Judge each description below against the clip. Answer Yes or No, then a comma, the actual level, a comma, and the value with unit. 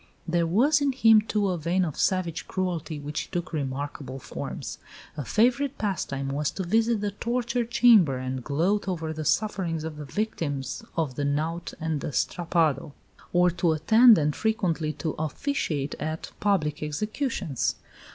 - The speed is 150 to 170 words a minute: Yes, average, 155 wpm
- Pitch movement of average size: No, wide, 5.9 semitones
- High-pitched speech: No, medium, 170 Hz